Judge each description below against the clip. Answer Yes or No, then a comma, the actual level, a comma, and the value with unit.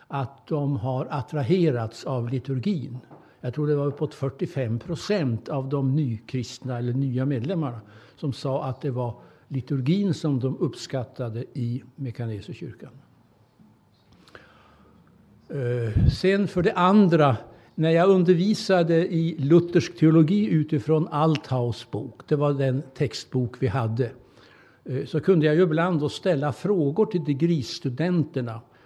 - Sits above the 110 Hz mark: Yes, medium, 140 Hz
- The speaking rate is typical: No, slow, 125 wpm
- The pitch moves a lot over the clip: No, average, 4.4 semitones